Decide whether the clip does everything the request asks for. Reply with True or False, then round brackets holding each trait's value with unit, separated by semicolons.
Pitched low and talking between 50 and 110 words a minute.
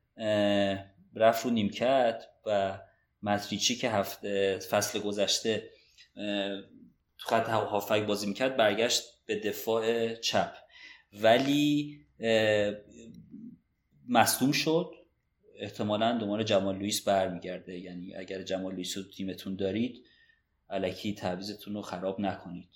True (105 Hz; 105 wpm)